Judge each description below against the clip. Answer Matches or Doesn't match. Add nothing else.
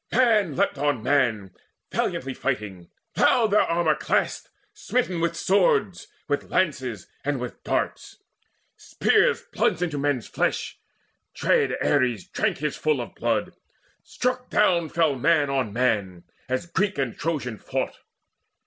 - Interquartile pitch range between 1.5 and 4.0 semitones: Doesn't match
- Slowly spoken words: Matches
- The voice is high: Doesn't match